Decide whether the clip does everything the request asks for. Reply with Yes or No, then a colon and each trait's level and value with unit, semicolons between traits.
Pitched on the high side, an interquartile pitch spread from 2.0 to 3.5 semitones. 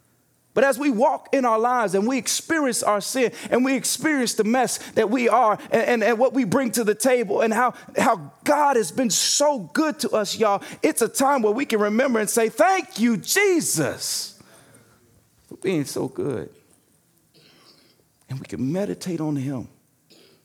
No: high, 240 Hz; average, 4.3 semitones